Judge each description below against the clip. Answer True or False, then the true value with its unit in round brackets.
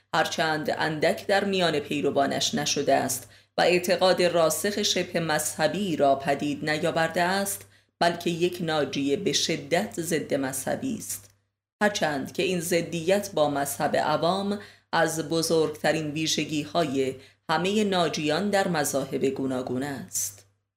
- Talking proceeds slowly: False (120 wpm)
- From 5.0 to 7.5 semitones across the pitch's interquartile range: False (4.0 semitones)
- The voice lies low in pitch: False (160 Hz)